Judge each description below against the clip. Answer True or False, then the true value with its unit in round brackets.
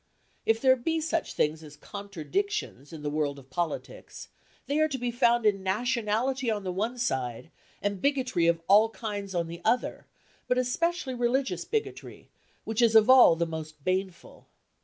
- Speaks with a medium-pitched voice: False (215 Hz)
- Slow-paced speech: False (170 wpm)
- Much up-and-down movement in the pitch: True (7.0 semitones)